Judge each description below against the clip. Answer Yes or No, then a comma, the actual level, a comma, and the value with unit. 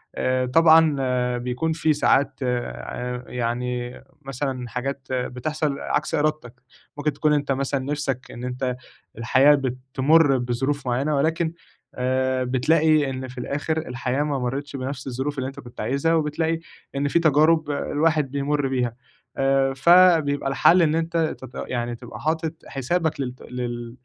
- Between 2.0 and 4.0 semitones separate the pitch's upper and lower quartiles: Yes, average, 3.2 semitones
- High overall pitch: No, low, 135 Hz